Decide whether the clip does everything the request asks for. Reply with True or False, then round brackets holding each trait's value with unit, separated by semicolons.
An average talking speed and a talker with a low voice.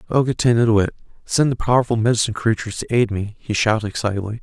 True (175 wpm; 110 Hz)